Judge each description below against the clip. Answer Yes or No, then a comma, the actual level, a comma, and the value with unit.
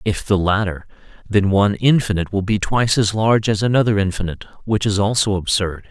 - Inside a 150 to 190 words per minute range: Yes, average, 185 wpm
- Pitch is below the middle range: Yes, low, 105 Hz